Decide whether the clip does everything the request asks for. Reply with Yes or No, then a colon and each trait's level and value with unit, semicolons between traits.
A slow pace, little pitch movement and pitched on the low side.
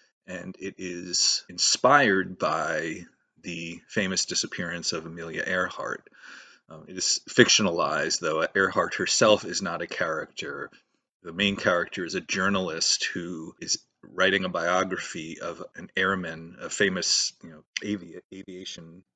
Yes: slow, 130 wpm; narrow, 2.3 semitones; very low, 90 Hz